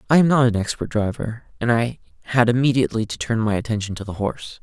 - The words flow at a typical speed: No, fast, 220 wpm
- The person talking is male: Yes, male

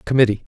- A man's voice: Yes, male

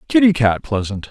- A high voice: No, medium, 140 Hz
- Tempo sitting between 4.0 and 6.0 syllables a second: Yes, 5.3 syllables/s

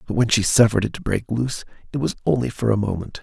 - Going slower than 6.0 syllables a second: No, 7.1 syllables/s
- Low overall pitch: Yes, low, 110 Hz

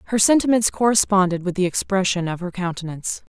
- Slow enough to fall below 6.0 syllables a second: No, 6.3 syllables/s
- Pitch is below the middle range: No, high, 190 Hz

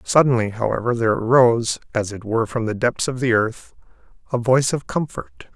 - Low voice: Yes, low, 120 Hz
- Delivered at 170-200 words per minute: Yes, average, 185 wpm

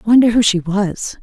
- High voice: Yes, high, 205 Hz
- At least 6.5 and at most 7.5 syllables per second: No, 5.8 syllables/s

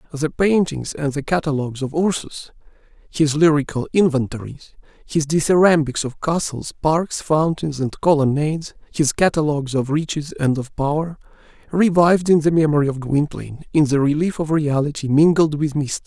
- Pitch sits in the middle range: Yes, medium, 150 Hz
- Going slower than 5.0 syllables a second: No, 5.2 syllables/s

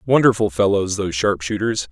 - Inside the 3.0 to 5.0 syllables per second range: No, 5.6 syllables/s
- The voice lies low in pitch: Yes, low, 100 Hz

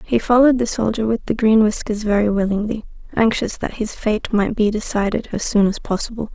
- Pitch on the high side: Yes, high, 215 Hz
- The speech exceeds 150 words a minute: Yes, average, 200 wpm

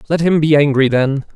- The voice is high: No, medium, 145 Hz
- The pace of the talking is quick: Yes, fast, 220 wpm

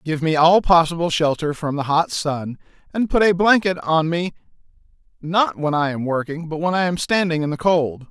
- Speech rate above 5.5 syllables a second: No, 5.0 syllables/s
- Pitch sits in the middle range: Yes, medium, 165 Hz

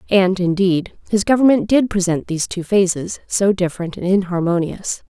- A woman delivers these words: Yes, female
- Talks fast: No, average, 155 wpm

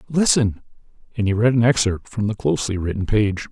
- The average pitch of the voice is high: No, low, 110 Hz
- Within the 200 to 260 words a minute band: No, average, 190 wpm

